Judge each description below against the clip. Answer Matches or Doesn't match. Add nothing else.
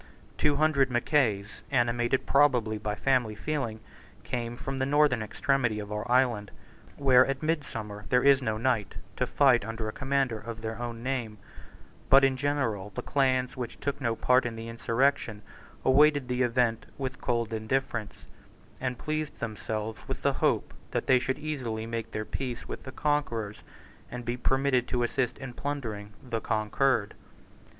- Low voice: Matches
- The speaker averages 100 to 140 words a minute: Doesn't match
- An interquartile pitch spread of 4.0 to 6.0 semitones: Doesn't match